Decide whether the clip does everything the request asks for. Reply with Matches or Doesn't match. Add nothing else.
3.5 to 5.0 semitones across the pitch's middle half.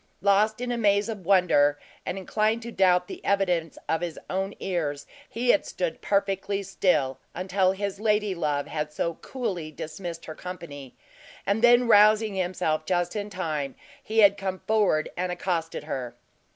Matches